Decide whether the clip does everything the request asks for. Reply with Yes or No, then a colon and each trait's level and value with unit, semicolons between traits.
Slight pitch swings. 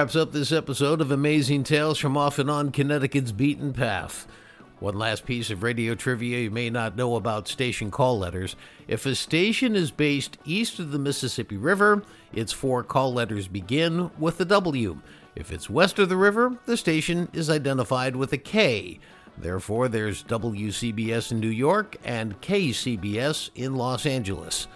No: average, 5.3 semitones